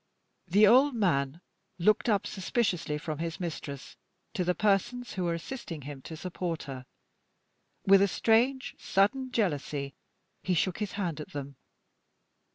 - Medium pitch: Yes, medium, 180 Hz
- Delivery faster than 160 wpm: No, average, 145 wpm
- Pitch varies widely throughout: Yes, wide, 5.7 semitones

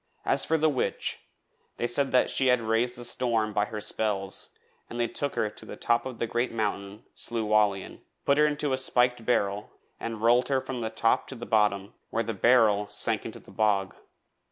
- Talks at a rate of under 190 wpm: No, average, 200 wpm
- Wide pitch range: No, average, 2.9 semitones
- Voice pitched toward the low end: Yes, low, 115 Hz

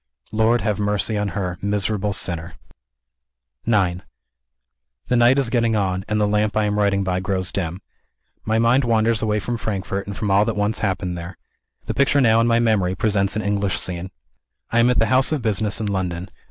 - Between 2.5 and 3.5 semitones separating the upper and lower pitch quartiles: Yes, average, 2.8 semitones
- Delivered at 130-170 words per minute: No, average, 195 wpm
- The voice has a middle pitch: No, low, 105 Hz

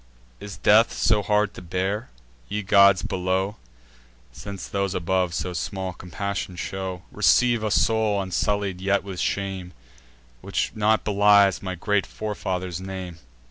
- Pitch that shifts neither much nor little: No, narrow, 1.9 semitones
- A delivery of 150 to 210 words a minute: No, slow, 135 wpm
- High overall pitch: No, very low, 95 Hz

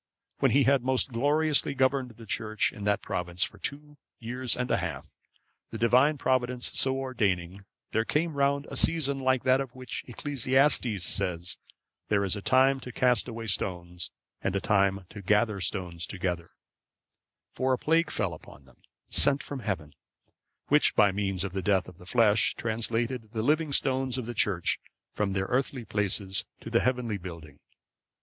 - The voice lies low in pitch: Yes, low, 115 Hz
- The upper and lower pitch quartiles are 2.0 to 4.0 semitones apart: No, average, 5.1 semitones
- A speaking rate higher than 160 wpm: Yes, average, 175 wpm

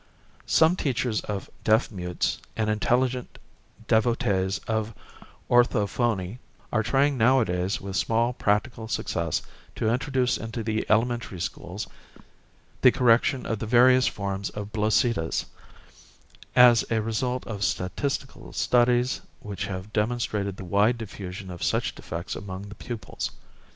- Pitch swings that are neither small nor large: Yes, average, 3.5 semitones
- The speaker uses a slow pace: Yes, slow, 125 wpm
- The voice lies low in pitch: Yes, low, 110 Hz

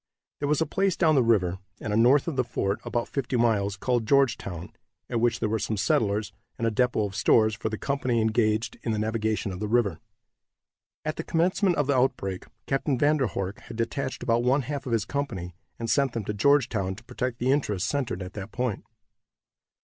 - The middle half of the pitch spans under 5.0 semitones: Yes, average, 4.3 semitones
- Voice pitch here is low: Yes, low, 115 Hz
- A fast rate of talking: Yes, fast, 210 wpm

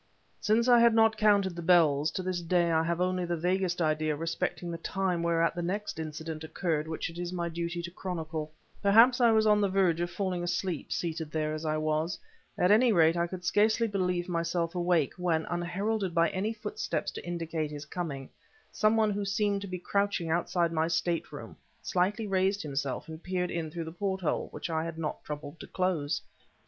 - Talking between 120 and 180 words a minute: No, average, 200 wpm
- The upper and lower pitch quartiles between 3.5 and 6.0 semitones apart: No, average, 3.0 semitones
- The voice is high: No, medium, 175 Hz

